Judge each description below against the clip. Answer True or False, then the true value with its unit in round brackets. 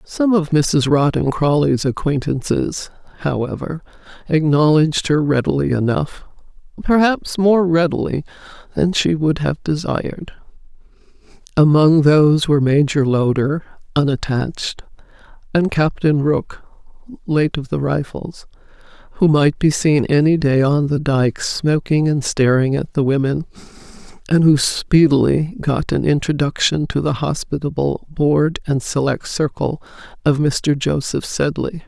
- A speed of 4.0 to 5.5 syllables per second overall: True (4.2 syllables/s)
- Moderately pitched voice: True (150 Hz)